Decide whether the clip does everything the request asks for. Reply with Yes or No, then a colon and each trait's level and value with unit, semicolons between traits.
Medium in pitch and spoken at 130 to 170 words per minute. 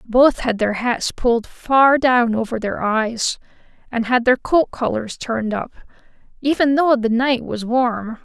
No: high, 240 Hz; average, 165 wpm